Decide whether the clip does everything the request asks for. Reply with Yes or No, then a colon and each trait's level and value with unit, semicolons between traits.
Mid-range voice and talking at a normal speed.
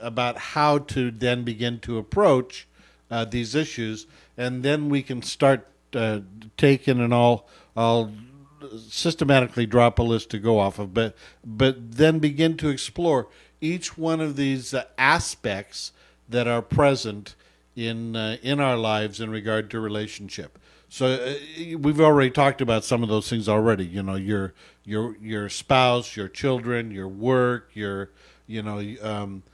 No: low, 120 Hz; average, 155 wpm